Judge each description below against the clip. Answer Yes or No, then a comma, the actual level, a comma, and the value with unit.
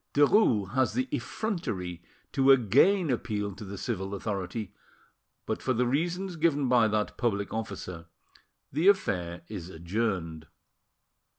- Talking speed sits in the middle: No, slow, 125 wpm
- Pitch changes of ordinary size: No, wide, 6.8 semitones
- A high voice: No, low, 110 Hz